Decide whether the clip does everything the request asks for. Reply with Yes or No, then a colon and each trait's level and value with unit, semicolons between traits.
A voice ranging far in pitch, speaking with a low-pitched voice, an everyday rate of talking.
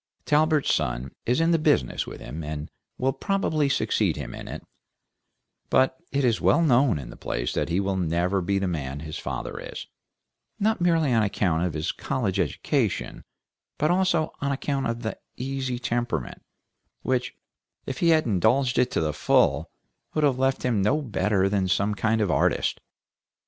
Yes: wide, 7.8 semitones; low, 115 Hz; average, 175 wpm